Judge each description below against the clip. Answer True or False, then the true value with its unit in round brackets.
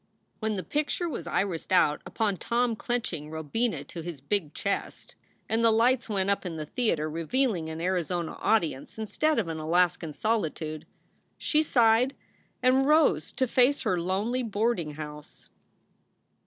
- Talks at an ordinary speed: True (155 wpm)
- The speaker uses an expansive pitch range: True (6.7 semitones)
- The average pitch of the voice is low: False (200 Hz)